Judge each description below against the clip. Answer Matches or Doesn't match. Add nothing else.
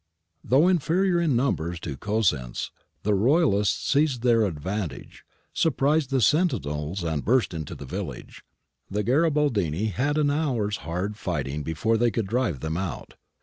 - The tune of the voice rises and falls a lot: Matches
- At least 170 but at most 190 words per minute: Doesn't match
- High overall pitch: Doesn't match